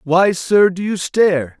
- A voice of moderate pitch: Yes, medium, 180 Hz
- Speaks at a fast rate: No, average, 190 wpm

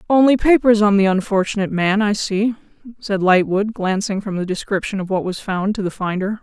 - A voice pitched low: No, high, 200 Hz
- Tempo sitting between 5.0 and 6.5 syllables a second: Yes, 5.5 syllables/s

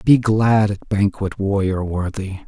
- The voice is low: Yes, low, 100 Hz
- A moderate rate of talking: Yes, average, 145 wpm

